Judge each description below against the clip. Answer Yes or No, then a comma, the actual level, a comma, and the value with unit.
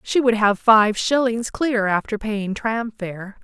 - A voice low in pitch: No, high, 220 Hz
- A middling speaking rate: Yes, average, 175 wpm